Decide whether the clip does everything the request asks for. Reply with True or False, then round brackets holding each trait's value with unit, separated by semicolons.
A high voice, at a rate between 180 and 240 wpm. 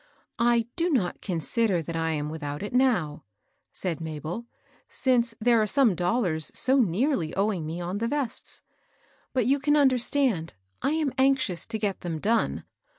False (215 Hz; 170 wpm)